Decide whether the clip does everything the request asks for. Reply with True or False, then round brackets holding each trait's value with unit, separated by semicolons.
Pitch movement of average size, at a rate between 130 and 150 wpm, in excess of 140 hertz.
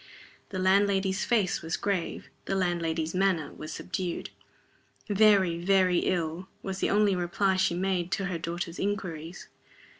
False (2.3 semitones; 140 wpm; 185 Hz)